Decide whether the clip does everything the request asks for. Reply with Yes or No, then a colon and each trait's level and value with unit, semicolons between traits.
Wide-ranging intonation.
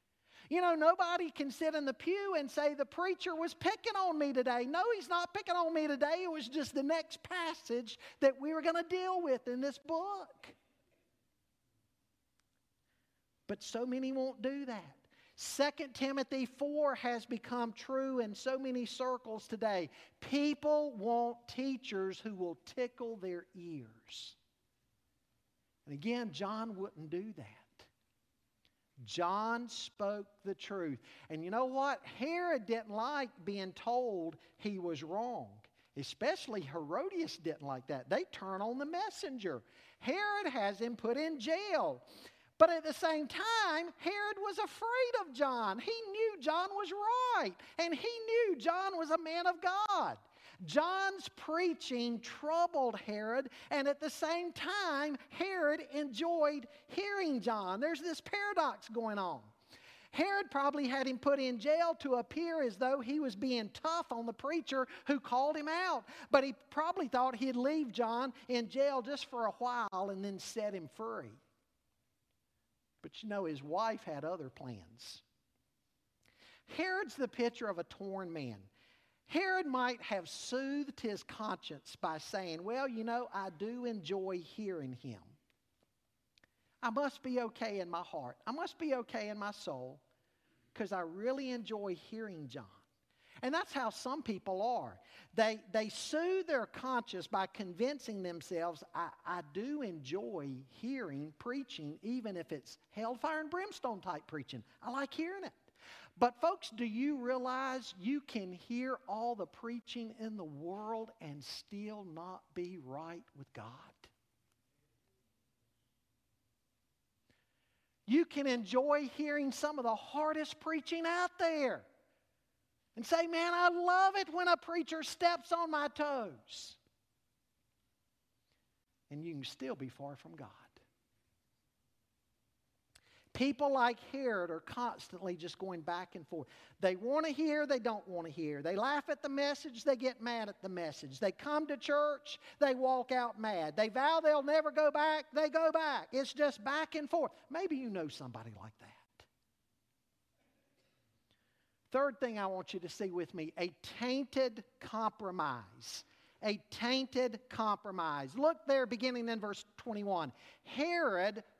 Yes: wide, 8.2 semitones